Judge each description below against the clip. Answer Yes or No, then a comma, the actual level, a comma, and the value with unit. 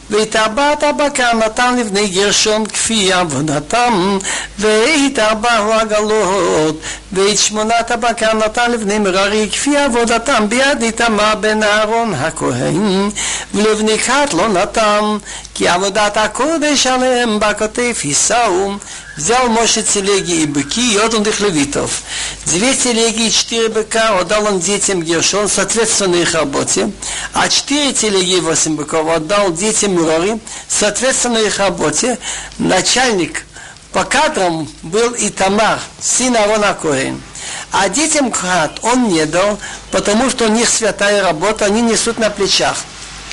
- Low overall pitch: No, high, 215 Hz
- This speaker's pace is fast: No, average, 125 wpm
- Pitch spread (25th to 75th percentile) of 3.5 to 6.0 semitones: No, average, 2.9 semitones